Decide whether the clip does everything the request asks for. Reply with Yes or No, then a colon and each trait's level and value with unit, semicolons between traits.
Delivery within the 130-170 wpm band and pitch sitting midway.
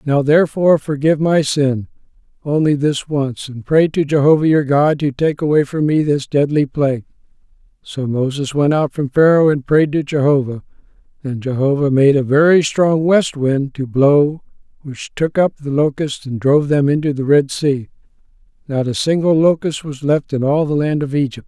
No: average, 185 wpm; medium, 145 Hz